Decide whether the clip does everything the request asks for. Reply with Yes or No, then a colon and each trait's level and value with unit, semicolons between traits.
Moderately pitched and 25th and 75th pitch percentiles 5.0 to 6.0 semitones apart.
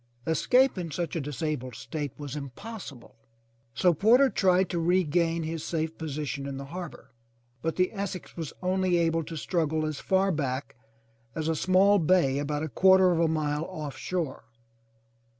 No: medium, 165 Hz; average, 3.7 semitones